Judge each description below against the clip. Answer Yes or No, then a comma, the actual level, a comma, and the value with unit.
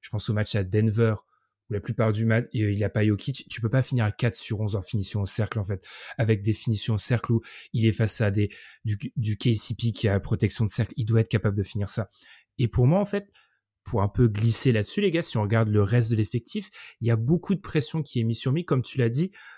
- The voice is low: Yes, low, 115 Hz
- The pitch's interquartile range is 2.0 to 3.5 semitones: Yes, narrow, 2.5 semitones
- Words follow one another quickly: Yes, fast, 280 wpm